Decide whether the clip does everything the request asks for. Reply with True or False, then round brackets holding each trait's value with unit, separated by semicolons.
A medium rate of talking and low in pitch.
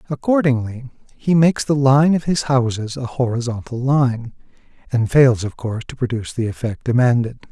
True (160 wpm; 125 Hz)